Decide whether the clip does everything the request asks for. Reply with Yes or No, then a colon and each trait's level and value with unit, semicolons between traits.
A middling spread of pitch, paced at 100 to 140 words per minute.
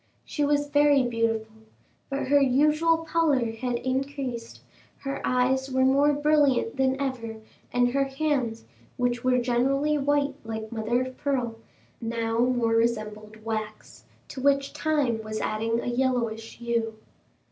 Yes: average, 3.5 semitones; slow, 135 wpm